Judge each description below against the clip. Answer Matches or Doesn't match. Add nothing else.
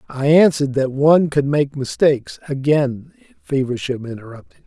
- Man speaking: Matches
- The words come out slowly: Matches